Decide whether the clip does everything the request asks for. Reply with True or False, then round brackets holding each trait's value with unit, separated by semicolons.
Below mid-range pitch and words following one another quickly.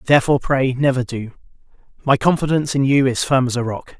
False (130 Hz; 195 wpm)